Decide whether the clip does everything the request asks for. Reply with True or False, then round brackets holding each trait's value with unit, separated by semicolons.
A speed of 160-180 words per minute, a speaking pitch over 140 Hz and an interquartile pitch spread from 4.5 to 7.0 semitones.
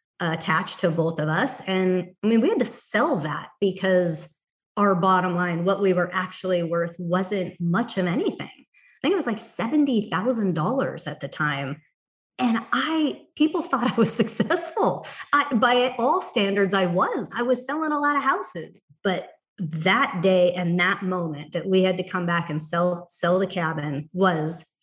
True (175 wpm; 185 Hz; 4.8 semitones)